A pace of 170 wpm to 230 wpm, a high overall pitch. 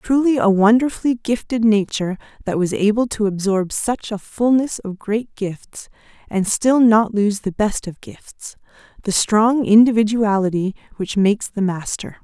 No: average, 145 wpm; high, 215 Hz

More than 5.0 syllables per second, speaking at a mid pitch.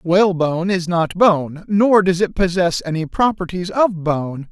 No: 4.3 syllables/s; medium, 180 Hz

